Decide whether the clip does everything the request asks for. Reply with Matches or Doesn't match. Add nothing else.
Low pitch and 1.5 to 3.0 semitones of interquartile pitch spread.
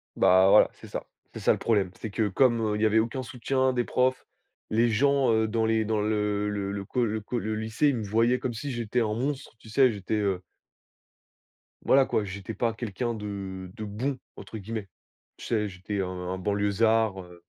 Matches